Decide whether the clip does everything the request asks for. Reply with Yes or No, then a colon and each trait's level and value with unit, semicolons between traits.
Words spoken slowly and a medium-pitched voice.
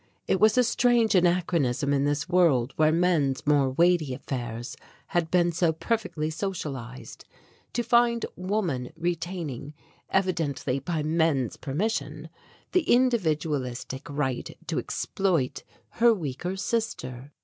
Yes: slow, 115 wpm; medium, 160 Hz